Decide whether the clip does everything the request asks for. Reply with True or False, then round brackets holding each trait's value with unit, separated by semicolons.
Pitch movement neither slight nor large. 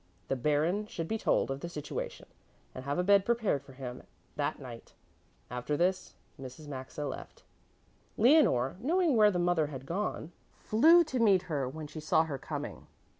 False (7.0 semitones)